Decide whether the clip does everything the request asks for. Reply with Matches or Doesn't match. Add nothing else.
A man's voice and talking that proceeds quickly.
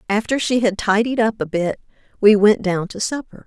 Doesn't match